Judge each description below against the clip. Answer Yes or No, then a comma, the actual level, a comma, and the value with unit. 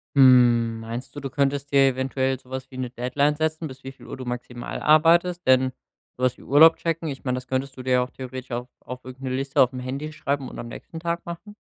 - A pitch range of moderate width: No, narrow, 2.3 semitones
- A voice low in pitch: Yes, low, 130 Hz